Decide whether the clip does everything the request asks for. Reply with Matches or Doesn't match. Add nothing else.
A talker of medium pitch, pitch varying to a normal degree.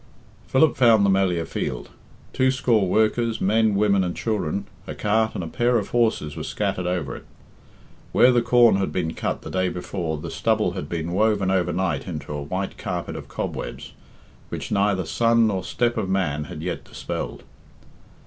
Doesn't match